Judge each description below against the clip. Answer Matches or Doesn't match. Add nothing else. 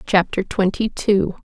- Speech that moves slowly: Matches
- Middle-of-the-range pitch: Doesn't match